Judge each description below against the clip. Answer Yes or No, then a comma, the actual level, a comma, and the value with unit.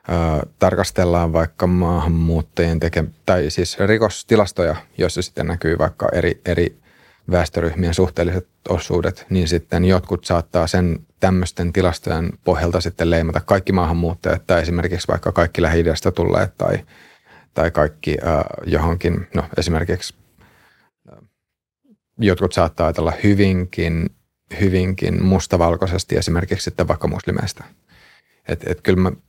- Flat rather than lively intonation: Yes, narrow, 1.8 semitones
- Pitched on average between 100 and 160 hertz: No, very low, 85 Hz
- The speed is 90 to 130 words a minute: Yes, average, 120 wpm